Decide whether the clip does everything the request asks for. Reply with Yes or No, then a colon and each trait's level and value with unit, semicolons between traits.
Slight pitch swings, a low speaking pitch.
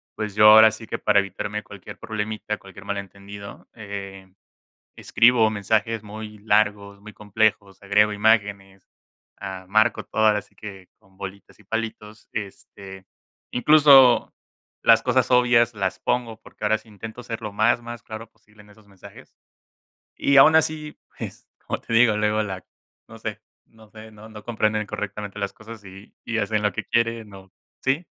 Yes: narrow, 1.8 semitones; low, 105 Hz